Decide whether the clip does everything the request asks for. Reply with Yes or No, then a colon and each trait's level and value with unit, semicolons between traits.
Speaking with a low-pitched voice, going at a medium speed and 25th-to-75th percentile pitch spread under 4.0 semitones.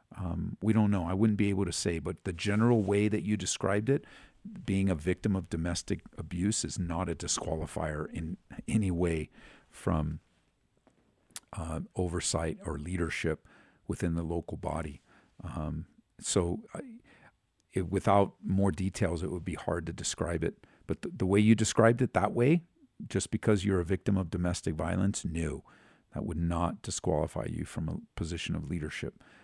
Yes: very low, 95 Hz; average, 165 wpm; average, 3.6 semitones